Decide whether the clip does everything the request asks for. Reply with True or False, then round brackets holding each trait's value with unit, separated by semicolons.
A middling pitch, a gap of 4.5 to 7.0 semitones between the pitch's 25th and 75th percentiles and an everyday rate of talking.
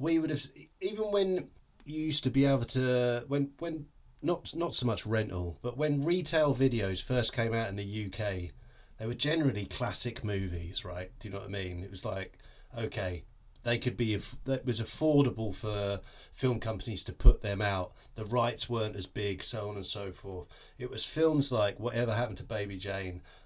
False (115 Hz; 5.1 semitones; 195 wpm)